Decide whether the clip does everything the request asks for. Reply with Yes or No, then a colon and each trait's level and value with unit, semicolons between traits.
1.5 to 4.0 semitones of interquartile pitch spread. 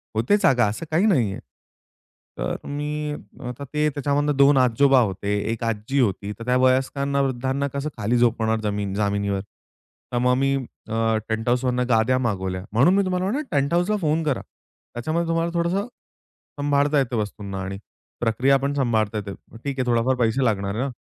No: average, 4.4 semitones